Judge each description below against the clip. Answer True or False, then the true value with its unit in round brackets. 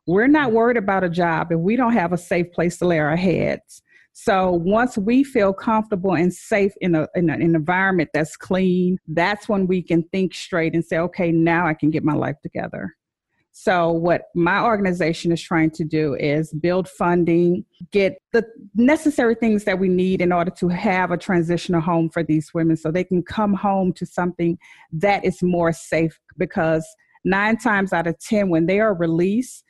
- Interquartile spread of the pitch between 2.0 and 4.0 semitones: True (3.1 semitones)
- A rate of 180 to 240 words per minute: True (200 wpm)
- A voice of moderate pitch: True (180 Hz)